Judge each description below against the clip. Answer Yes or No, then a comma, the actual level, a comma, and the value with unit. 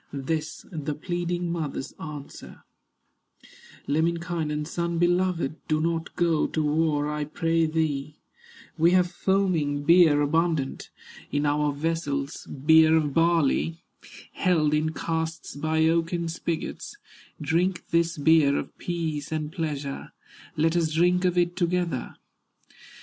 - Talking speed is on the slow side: Yes, slow, 120 wpm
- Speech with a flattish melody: Yes, narrow, 2.2 semitones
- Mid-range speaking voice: Yes, medium, 160 Hz